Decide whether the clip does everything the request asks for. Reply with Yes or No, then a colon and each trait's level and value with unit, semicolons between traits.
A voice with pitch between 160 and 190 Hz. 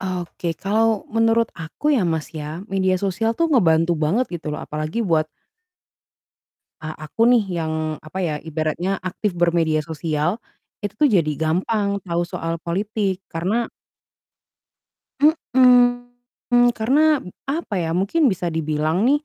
Yes: medium, 185 Hz